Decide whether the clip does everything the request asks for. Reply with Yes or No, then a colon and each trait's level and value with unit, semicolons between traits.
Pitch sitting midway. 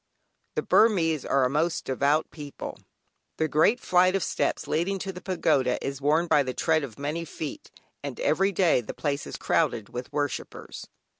Yes: medium, 155 Hz